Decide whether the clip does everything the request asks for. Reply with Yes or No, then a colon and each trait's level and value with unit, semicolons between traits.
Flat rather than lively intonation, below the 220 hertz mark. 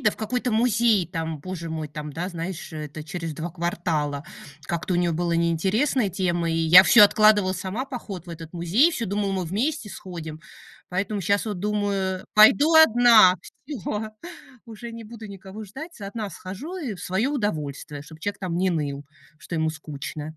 No: average, 4.6 semitones; medium, 185 Hz